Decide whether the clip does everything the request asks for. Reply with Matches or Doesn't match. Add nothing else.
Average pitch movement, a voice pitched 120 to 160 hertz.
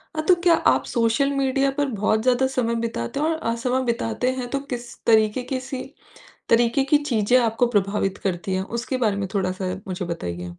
Doesn't match